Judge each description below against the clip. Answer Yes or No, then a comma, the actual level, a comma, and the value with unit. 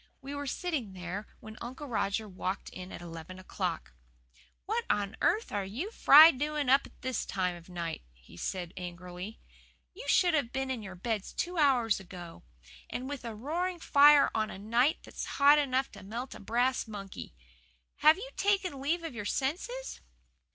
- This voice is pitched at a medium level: No, high, 240 Hz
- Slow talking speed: No, average, 180 wpm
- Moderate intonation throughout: No, wide, 7.3 semitones